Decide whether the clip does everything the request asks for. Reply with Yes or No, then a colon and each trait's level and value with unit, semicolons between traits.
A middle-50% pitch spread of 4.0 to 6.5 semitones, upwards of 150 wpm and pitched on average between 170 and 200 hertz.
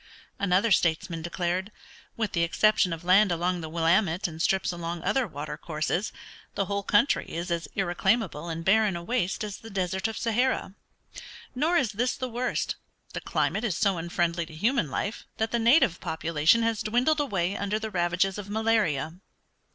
Yes: average, 4.5 semitones; average, 175 wpm; high, 190 Hz